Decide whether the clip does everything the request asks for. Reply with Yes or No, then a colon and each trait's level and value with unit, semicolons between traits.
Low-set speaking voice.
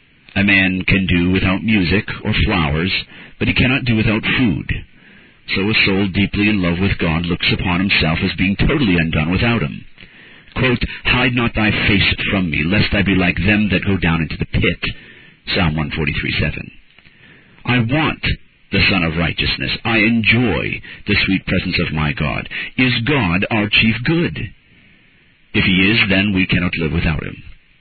Yes: very low, 95 Hz